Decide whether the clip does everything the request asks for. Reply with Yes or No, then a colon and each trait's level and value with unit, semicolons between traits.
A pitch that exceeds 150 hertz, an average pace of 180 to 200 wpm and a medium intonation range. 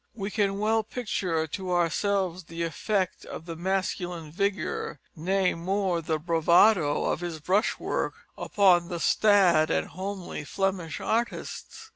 No: medium, 185 Hz; slow, 135 wpm; average, 3.1 semitones